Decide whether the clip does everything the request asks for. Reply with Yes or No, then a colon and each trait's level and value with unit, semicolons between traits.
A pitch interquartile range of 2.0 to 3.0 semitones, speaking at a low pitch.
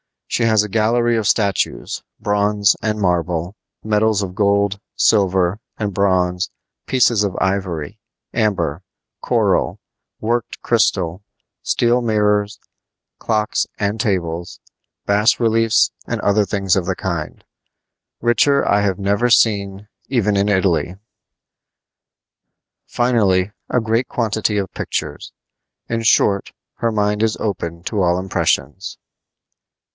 Yes: average, 2.7 semitones; low, 100 Hz